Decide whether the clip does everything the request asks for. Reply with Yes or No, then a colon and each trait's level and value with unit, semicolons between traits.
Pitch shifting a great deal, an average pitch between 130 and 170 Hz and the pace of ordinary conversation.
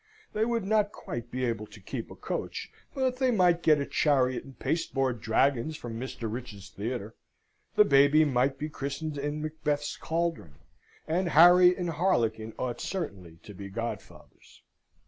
Yes: wide, 6.4 semitones; medium, 140 Hz; average, 160 wpm